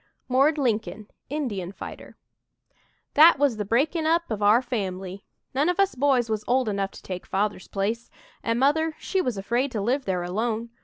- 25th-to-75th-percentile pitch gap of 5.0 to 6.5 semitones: Yes, wide, 5.6 semitones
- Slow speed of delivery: No, average, 175 wpm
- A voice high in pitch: Yes, high, 235 Hz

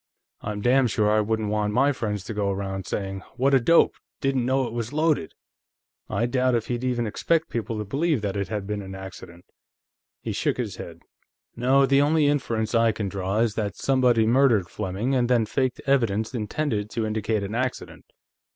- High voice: No, low, 115 Hz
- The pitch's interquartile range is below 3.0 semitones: No, average, 3.9 semitones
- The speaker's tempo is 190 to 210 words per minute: Yes, average, 195 wpm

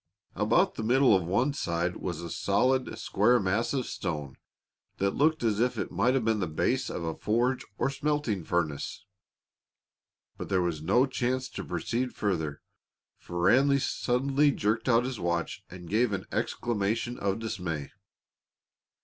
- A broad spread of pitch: Yes, wide, 6.2 semitones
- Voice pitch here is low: Yes, low, 110 Hz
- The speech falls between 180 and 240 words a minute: No, average, 160 wpm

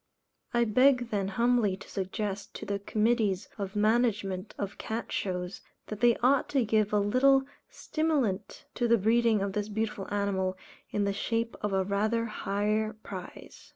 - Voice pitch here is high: Yes, high, 210 Hz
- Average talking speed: Yes, average, 160 wpm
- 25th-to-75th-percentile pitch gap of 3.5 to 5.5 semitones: No, average, 2.8 semitones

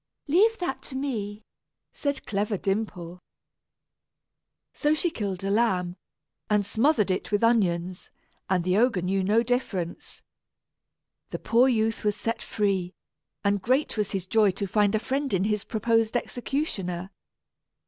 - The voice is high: Yes, high, 210 Hz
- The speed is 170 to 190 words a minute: No, average, 140 wpm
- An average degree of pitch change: Yes, average, 3.9 semitones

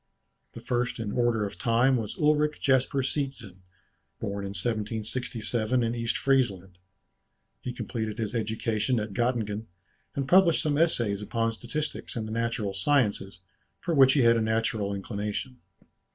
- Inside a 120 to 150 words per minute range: Yes, average, 145 wpm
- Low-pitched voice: Yes, low, 115 Hz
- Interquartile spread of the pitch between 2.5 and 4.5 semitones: Yes, average, 3.6 semitones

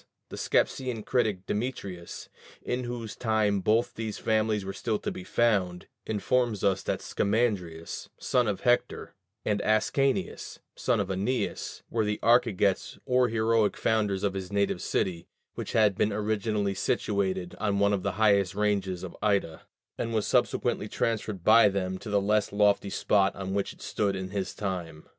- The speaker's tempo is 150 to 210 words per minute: Yes, average, 160 wpm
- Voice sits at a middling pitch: No, low, 105 Hz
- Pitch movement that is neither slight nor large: No, narrow, 2.3 semitones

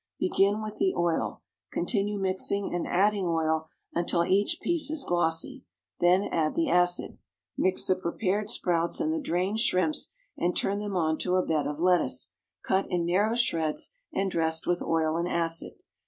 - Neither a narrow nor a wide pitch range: Yes, average, 3.2 semitones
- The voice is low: No, medium, 180 Hz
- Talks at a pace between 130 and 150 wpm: No, average, 165 wpm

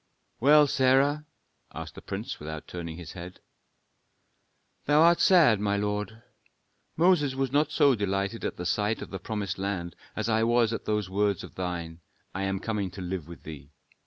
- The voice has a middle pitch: No, low, 105 Hz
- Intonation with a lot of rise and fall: Yes, wide, 6.1 semitones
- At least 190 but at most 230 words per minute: No, average, 170 wpm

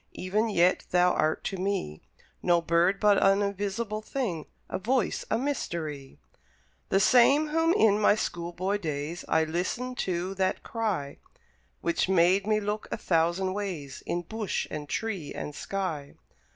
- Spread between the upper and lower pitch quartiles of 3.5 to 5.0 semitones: Yes, average, 3.9 semitones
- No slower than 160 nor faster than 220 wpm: No, average, 150 wpm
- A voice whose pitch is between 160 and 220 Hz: Yes, high, 190 Hz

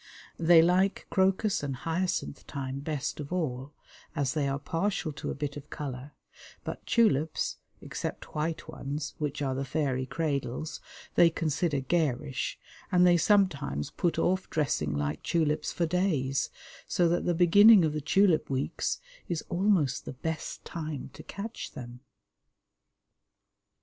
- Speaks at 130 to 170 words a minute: Yes, average, 145 wpm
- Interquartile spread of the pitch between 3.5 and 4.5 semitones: Yes, average, 4.2 semitones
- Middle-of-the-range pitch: Yes, medium, 155 Hz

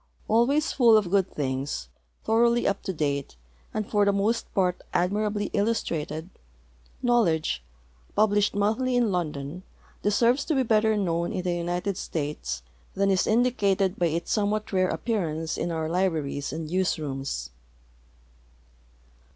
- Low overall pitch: No, high, 190 Hz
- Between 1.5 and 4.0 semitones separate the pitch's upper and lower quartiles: No, average, 5.1 semitones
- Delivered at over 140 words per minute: No, slow, 135 wpm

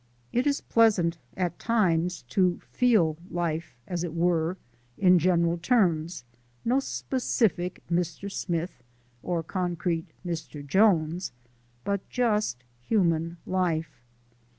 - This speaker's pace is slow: Yes, slow, 105 wpm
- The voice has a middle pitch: Yes, medium, 175 Hz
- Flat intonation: No, average, 3.1 semitones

